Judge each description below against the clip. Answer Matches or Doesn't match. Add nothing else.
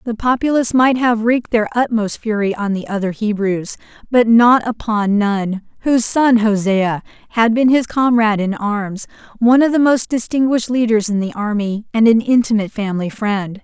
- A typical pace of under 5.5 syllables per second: Matches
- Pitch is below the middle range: Doesn't match